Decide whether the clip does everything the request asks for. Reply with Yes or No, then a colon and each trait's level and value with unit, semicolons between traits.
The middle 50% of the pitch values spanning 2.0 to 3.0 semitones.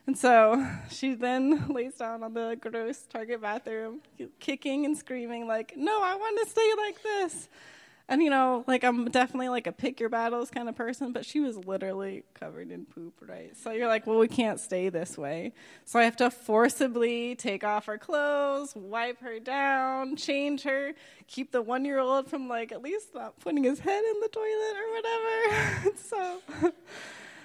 No: average, 4.5 semitones